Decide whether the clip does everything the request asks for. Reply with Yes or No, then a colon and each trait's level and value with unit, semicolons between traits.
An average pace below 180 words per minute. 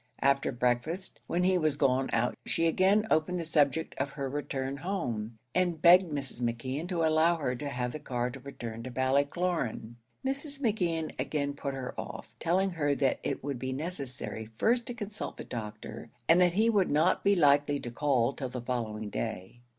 No: average, 190 wpm